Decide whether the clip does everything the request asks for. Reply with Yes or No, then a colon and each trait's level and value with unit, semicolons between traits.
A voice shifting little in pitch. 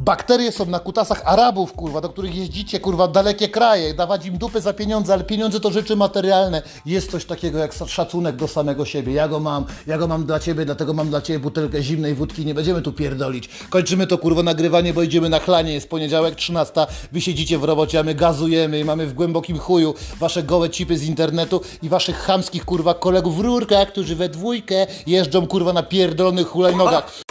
No: average, 3.1 semitones